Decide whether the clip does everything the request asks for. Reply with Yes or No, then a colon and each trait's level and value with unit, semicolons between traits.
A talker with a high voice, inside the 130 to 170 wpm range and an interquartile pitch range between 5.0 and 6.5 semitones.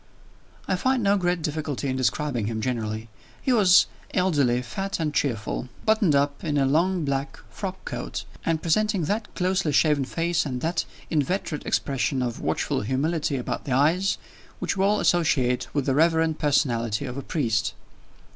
No: medium, 150 Hz; average, 160 wpm; wide, 5.4 semitones